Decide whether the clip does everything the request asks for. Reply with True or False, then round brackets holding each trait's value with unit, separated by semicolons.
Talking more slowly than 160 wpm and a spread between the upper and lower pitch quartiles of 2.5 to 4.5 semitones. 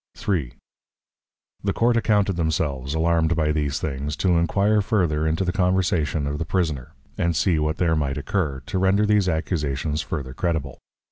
False (165 wpm; 4.1 semitones)